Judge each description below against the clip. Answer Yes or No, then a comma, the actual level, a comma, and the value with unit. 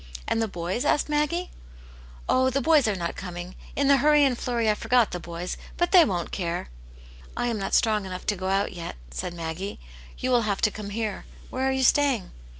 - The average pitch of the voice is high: Yes, high, 215 Hz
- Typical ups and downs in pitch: No, wide, 6.4 semitones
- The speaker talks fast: Yes, fast, 235 wpm